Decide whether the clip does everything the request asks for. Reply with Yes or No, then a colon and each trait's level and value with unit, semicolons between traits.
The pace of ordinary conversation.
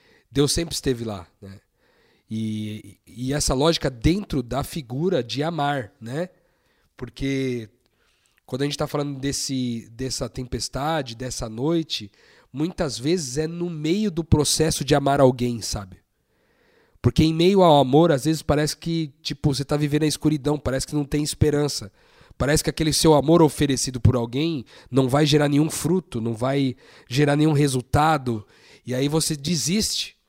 Yes: average, 155 wpm